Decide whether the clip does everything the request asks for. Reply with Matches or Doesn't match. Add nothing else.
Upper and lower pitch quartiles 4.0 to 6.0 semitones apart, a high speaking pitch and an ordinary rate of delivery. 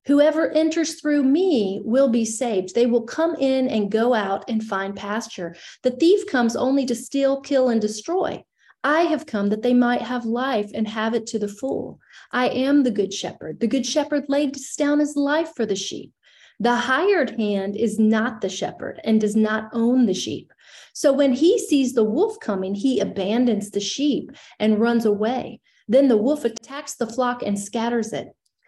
Matches